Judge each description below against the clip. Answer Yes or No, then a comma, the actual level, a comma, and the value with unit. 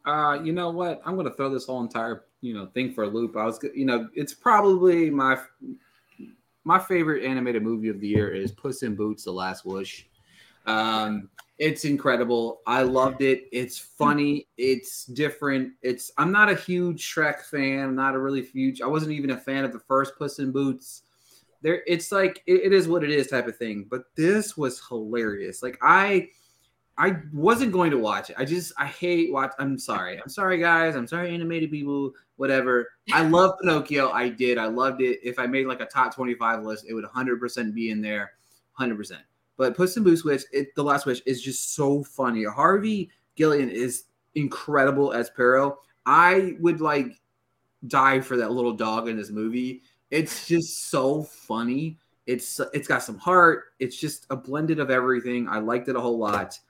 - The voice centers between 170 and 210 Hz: No, low, 135 Hz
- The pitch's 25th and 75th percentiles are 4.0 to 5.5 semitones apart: Yes, average, 4.3 semitones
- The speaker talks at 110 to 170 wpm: No, average, 195 wpm